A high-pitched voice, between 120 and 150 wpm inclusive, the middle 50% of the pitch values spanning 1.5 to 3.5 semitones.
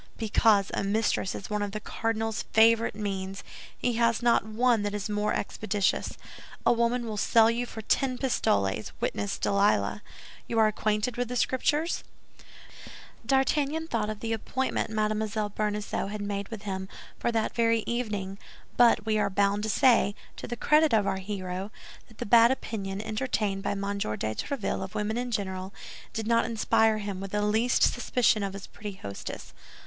No: high, 215 Hz; average, 175 wpm; narrow, 2.5 semitones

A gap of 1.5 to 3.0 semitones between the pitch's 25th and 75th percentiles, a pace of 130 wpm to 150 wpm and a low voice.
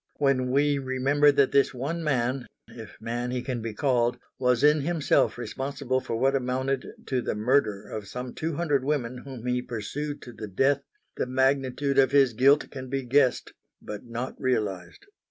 No: narrow, 2.5 semitones; average, 175 wpm; low, 130 Hz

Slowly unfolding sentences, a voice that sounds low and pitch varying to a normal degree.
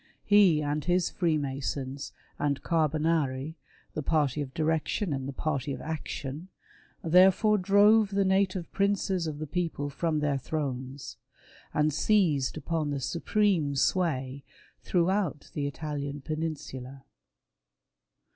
No: slow, 125 wpm; medium, 155 Hz; average, 4.0 semitones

